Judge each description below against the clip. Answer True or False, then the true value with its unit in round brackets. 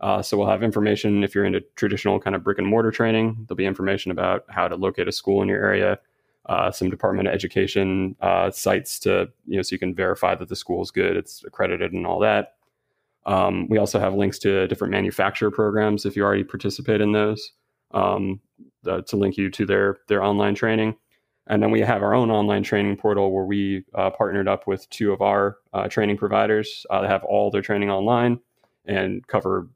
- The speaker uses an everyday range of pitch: False (1.5 semitones)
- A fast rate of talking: True (215 wpm)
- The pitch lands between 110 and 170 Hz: False (100 Hz)